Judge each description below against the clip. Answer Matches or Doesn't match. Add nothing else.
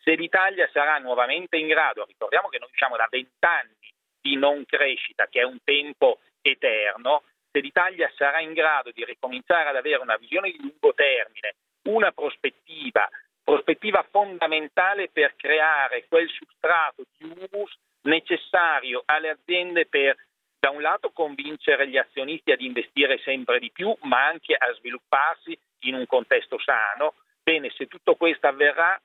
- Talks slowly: Doesn't match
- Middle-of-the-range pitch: Matches